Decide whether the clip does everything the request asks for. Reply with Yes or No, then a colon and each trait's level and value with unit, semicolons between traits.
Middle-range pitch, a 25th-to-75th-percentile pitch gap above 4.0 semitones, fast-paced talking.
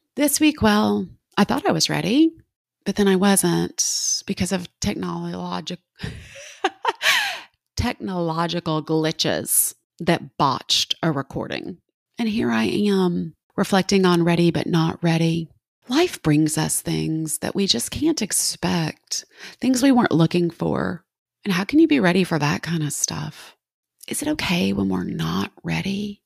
No: medium, 175 Hz; average, 4.6 semitones; average, 145 wpm